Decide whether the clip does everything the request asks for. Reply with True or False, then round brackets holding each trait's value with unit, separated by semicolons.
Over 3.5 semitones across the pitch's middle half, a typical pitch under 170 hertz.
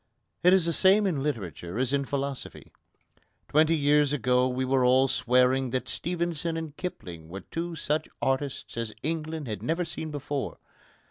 True (4.2 semitones; 140 Hz)